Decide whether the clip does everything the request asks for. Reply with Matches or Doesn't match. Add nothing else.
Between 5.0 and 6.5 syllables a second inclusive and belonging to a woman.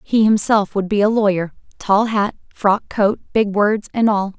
Doesn't match